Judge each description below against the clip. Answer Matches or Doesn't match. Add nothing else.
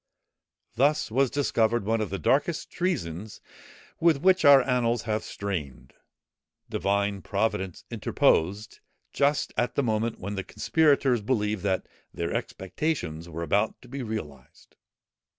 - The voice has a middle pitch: Doesn't match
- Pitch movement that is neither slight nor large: Doesn't match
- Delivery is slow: Matches